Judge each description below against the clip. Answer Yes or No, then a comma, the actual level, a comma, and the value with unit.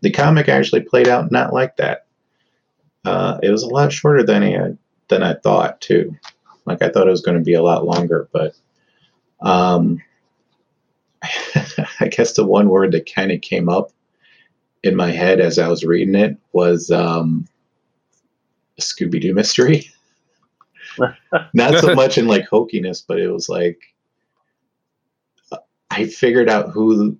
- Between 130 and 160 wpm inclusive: Yes, average, 155 wpm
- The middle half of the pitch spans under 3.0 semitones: No, average, 3.5 semitones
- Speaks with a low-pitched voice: Yes, very low, 90 Hz